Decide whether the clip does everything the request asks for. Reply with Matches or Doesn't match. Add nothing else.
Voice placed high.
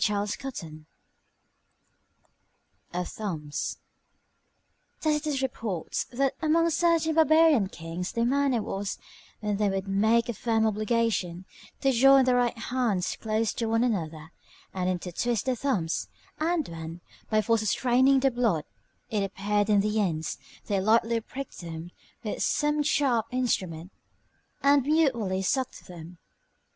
Matches